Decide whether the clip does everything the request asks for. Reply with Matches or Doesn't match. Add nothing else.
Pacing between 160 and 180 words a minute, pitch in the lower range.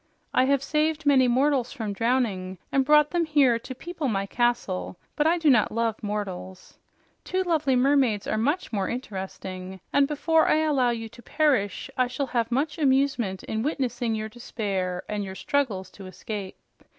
Doesn't match